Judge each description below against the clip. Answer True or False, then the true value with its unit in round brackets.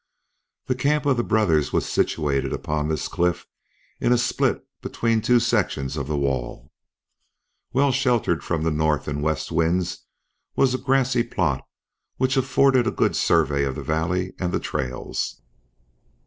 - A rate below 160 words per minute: True (150 wpm)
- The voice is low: True (90 Hz)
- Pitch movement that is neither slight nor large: False (8.5 semitones)